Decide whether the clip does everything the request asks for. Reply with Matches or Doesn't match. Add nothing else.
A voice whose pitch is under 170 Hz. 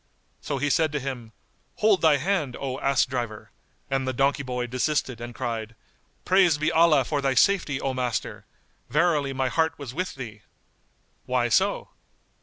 Matches